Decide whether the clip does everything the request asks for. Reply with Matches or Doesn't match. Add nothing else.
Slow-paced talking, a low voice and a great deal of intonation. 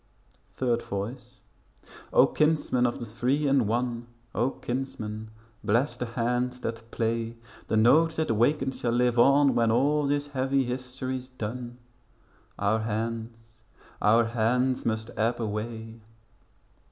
Doesn't match